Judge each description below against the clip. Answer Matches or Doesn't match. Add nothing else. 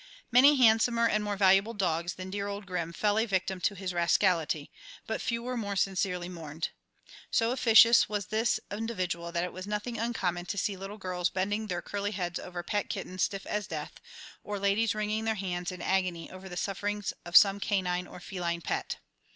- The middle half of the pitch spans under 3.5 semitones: Matches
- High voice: Matches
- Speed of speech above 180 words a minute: Matches